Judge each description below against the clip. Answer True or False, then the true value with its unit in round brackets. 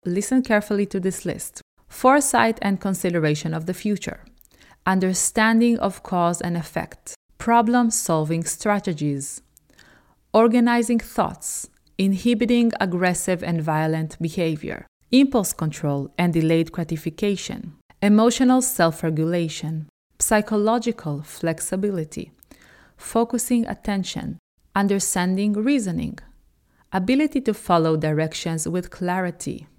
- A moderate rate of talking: False (95 wpm)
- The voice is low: False (185 Hz)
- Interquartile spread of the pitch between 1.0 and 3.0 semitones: False (5.4 semitones)